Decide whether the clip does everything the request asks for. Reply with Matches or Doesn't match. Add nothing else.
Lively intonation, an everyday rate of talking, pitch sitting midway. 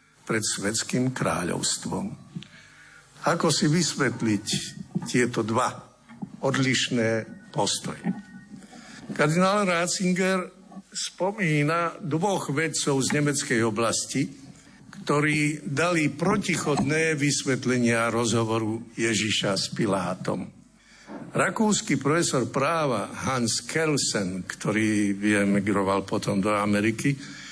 Doesn't match